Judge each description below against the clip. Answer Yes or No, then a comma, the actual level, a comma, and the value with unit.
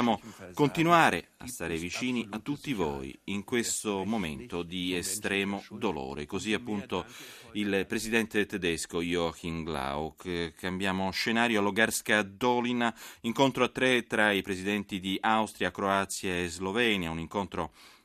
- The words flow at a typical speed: Yes, average, 125 wpm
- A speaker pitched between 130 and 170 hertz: No, low, 100 Hz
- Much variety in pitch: No, average, 4.0 semitones